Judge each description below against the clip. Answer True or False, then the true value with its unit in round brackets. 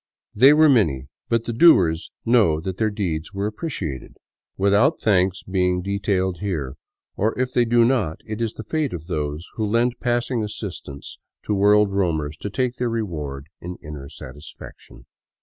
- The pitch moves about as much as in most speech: False (6.1 semitones)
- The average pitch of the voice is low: True (100 Hz)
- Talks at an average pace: True (165 wpm)